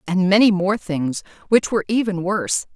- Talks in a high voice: Yes, high, 195 Hz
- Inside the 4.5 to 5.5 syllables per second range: Yes, 5.3 syllables/s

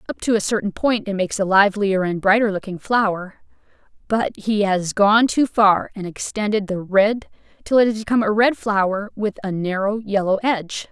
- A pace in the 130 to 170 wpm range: No, average, 190 wpm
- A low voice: No, high, 205 Hz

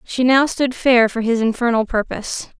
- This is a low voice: No, high, 240 Hz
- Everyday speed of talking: Yes, average, 185 wpm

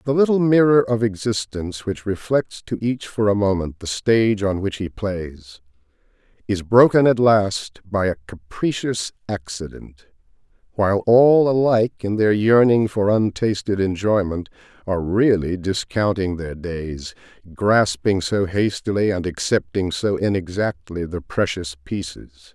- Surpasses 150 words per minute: No, slow, 135 wpm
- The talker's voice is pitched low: Yes, low, 100 Hz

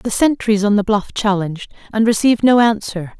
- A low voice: No, high, 210 Hz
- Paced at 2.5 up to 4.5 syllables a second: No, 5.5 syllables/s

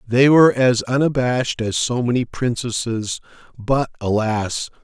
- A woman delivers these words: No, male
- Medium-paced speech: No, slow, 125 wpm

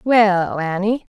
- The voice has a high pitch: Yes, high, 200 Hz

